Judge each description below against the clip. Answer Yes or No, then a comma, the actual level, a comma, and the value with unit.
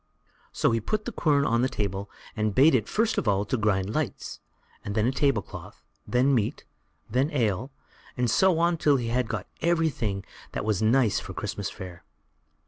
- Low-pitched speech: Yes, low, 120 Hz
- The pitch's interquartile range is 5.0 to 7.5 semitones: Yes, wide, 5.4 semitones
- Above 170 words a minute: Yes, average, 180 wpm